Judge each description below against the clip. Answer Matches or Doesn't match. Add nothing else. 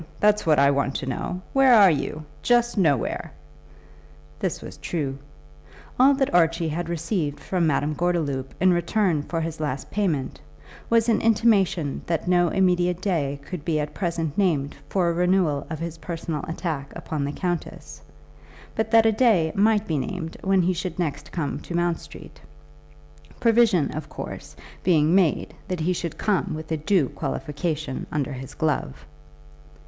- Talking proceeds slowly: Doesn't match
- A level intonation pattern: Doesn't match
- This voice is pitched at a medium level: Matches